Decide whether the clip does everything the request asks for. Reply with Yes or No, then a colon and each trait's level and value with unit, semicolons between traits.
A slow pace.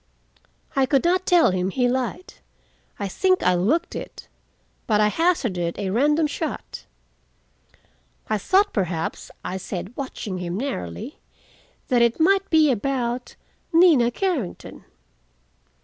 Yes: slow, 120 wpm